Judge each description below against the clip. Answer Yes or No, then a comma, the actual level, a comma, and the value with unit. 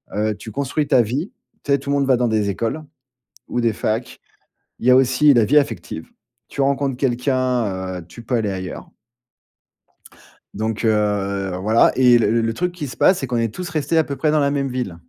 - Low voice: Yes, low, 120 Hz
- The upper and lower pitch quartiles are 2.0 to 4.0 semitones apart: No, average, 4.5 semitones